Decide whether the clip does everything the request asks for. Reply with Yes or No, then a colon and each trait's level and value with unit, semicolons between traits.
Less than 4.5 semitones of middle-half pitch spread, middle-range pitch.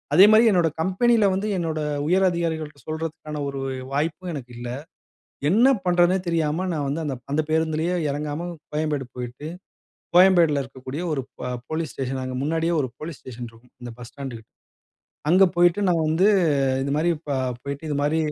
Yes: average, 3.8 semitones; medium, 155 Hz